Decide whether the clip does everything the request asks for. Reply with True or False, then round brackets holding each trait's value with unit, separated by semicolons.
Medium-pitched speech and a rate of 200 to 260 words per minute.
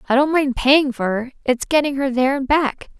False (270 Hz; 240 wpm)